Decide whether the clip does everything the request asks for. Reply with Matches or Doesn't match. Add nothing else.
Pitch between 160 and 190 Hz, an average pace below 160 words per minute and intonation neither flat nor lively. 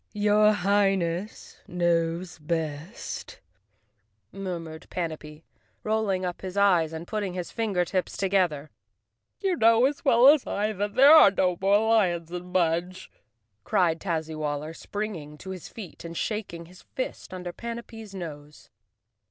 Matches